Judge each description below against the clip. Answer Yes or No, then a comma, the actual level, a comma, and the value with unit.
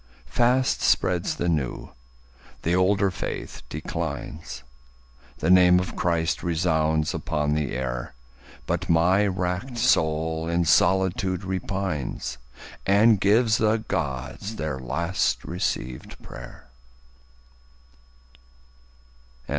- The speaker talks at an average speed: No, slow, 95 wpm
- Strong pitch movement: No, average, 3.8 semitones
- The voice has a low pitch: Yes, very low, 85 Hz